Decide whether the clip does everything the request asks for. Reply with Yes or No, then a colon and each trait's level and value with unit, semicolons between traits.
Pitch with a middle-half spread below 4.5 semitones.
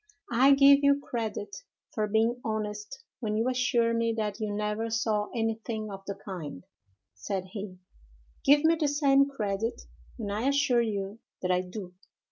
Yes: average, 3.3 semitones